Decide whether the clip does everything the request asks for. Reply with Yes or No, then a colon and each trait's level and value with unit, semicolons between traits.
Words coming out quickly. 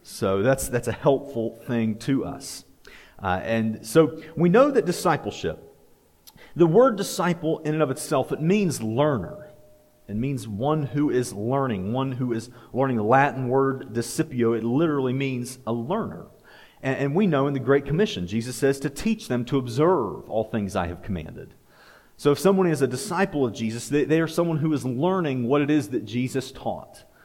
No: average, 185 wpm